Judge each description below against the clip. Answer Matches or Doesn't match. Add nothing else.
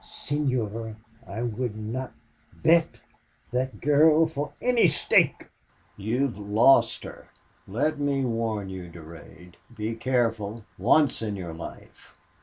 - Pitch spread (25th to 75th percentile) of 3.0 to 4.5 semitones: Doesn't match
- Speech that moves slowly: Matches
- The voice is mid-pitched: Doesn't match